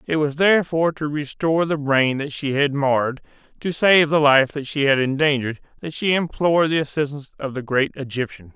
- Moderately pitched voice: Yes, medium, 145 Hz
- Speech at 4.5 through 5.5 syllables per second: No, 5.7 syllables/s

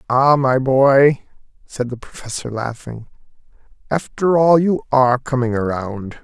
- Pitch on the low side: Yes, low, 130 Hz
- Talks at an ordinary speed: No, slow, 125 wpm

